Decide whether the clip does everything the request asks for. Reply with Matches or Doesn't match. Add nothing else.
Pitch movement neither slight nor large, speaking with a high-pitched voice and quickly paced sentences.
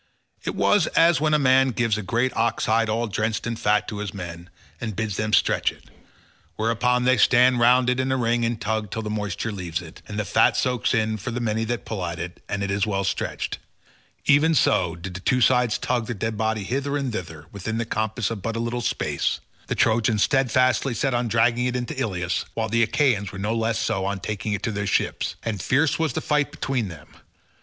Doesn't match